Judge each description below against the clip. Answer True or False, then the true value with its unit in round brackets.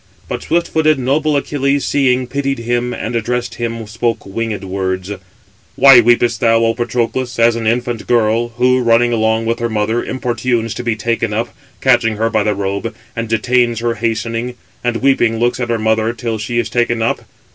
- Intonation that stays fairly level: True (1.5 semitones)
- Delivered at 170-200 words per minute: True (185 wpm)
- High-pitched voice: False (115 Hz)